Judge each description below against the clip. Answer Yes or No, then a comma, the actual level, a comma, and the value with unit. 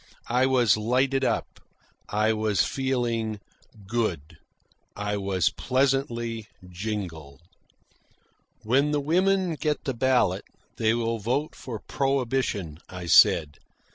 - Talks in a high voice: No, low, 115 Hz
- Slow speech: Yes, slow, 110 wpm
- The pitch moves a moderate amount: Yes, average, 4.5 semitones